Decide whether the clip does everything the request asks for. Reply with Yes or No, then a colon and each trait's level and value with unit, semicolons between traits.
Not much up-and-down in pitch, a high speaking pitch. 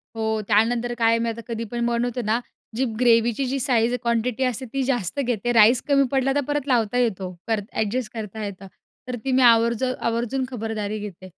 Yes: narrow, 2.3 semitones; high, 235 Hz